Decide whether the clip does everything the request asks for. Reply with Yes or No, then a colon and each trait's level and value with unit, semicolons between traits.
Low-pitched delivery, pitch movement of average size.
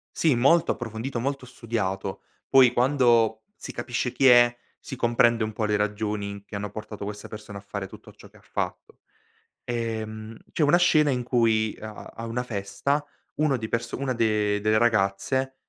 Yes: low, 115 Hz; average, 3.0 semitones